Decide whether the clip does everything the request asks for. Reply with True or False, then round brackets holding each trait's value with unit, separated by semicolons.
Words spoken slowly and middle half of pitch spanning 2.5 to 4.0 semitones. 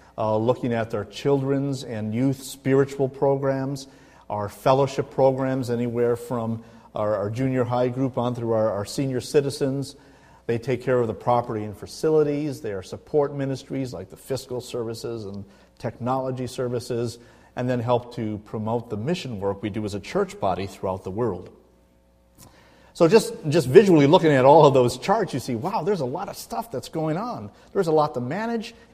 False (190 wpm; 3.5 semitones)